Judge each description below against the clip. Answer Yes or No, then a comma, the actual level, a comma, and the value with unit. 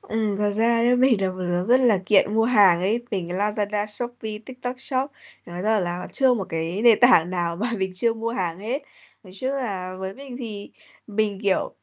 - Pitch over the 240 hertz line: No, high, 210 Hz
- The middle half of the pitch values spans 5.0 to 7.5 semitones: No, average, 4.2 semitones